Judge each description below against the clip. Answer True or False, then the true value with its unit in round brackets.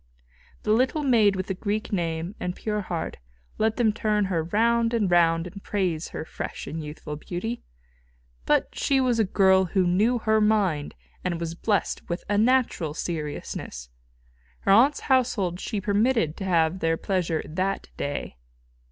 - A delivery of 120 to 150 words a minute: False (160 wpm)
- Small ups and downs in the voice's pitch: False (4.6 semitones)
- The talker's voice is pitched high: True (195 Hz)